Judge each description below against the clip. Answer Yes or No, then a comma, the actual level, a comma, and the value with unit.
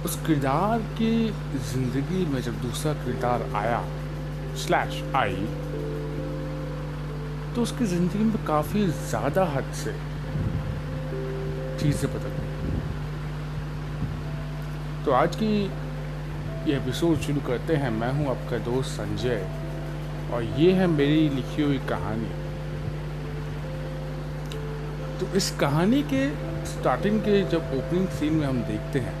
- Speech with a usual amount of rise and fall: Yes, average, 4.4 semitones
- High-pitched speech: No, medium, 150 Hz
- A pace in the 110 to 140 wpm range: Yes, average, 115 wpm